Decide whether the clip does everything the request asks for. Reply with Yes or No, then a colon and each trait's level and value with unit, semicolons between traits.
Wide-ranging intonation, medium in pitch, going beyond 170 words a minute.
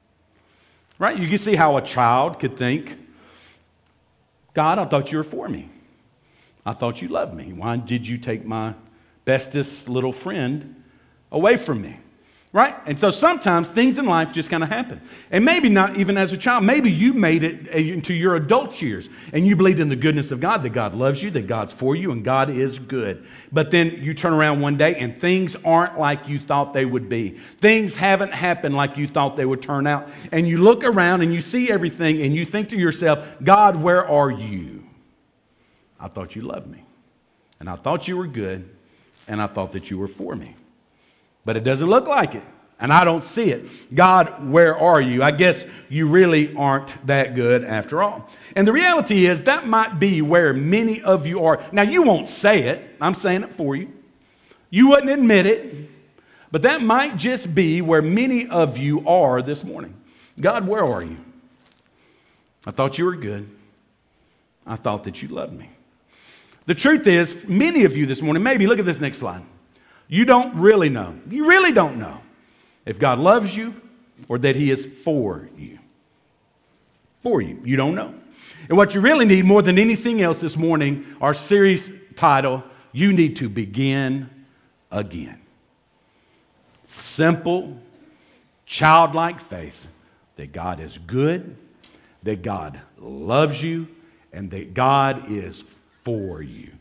Yes: wide, 6.6 semitones; medium, 155 Hz; average, 180 wpm